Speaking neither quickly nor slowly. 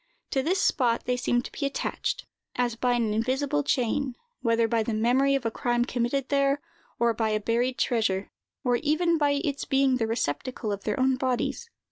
Yes: average, 190 wpm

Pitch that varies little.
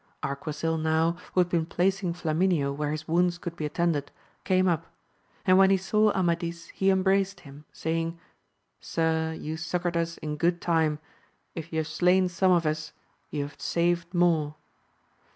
Yes: narrow, 2.1 semitones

